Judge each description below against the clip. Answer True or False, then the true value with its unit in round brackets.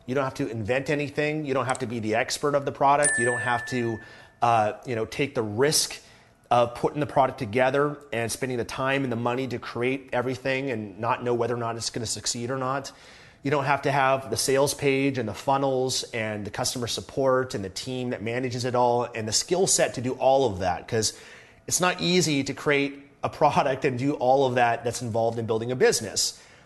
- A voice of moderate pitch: False (130 Hz)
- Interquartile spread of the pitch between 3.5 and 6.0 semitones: False (2.8 semitones)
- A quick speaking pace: True (230 wpm)